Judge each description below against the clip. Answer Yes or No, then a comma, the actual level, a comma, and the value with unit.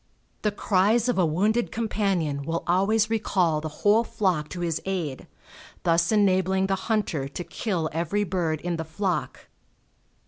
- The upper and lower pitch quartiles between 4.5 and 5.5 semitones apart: No, average, 4.1 semitones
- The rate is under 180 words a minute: Yes, average, 150 wpm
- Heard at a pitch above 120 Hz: Yes, medium, 185 Hz